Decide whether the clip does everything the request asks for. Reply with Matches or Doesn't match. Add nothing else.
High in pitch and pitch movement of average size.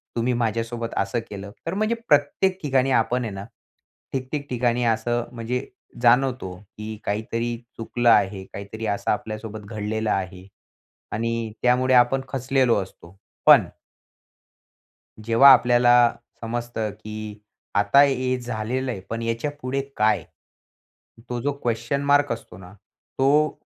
Doesn't match